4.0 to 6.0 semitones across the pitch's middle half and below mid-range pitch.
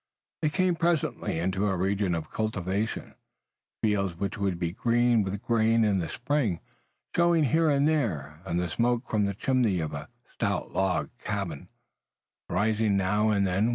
Yes: average, 4.3 semitones; low, 105 Hz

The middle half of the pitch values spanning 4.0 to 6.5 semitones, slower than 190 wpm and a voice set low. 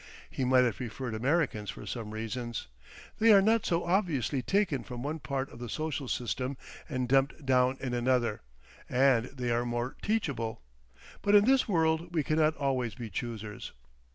Yes: average, 4.8 semitones; average, 170 wpm; low, 130 Hz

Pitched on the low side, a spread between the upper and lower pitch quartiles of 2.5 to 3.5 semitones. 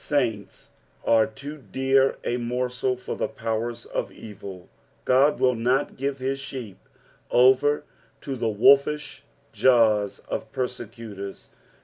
Yes: low, 125 Hz; average, 3.2 semitones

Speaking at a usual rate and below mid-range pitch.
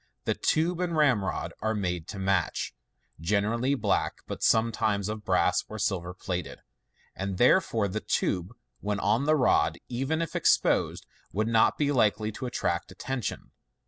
Yes: average, 150 wpm; low, 110 Hz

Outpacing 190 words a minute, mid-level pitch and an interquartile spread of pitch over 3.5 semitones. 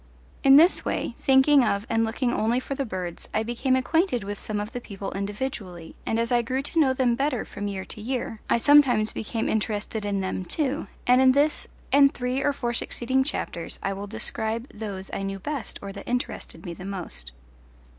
No: fast, 205 wpm; high, 230 Hz; average, 4.6 semitones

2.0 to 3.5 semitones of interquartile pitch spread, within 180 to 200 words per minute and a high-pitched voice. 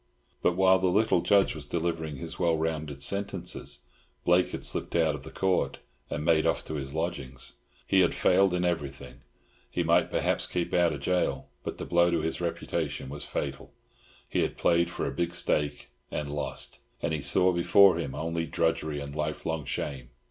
No: average, 3.0 semitones; average, 185 wpm; very low, 80 Hz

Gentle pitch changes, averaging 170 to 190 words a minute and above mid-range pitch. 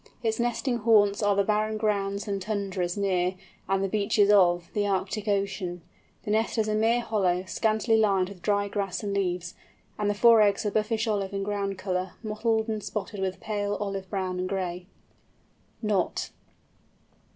Yes: narrow, 2.0 semitones; average, 175 wpm; high, 200 Hz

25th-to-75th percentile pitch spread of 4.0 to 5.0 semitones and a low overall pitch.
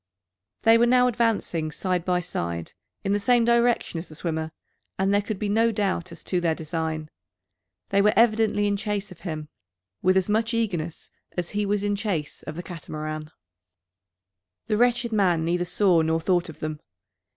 No: average, 4.7 semitones; high, 190 Hz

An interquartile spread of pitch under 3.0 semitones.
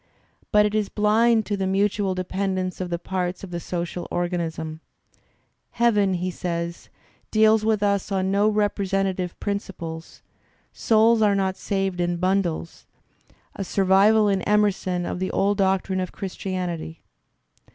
Yes: narrow, 2.4 semitones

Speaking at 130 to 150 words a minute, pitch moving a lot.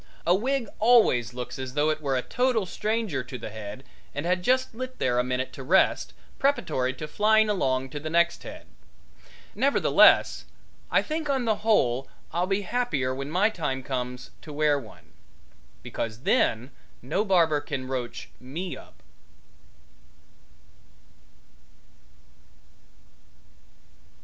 Yes: slow, 135 wpm; wide, 8.7 semitones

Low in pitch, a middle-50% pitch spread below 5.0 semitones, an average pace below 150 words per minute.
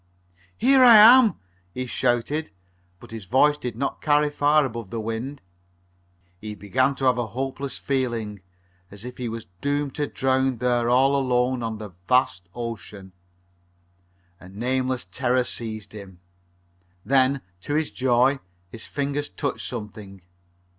Yes: low, 125 Hz; average, 3.7 semitones; average, 140 wpm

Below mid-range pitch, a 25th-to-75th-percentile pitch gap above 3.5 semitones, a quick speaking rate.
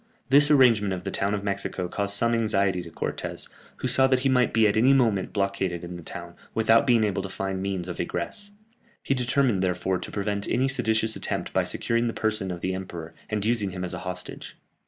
Yes: low, 100 Hz; average, 3.9 semitones; fast, 220 wpm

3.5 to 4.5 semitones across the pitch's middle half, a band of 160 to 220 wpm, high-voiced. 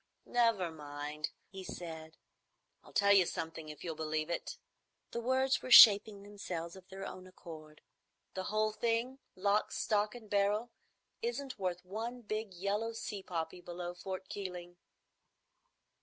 No: average, 3.9 semitones; average, 140 wpm; high, 195 Hz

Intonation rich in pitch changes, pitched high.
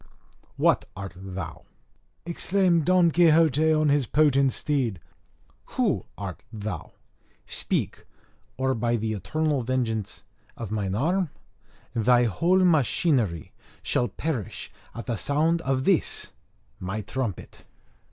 No: wide, 6.7 semitones; low, 130 Hz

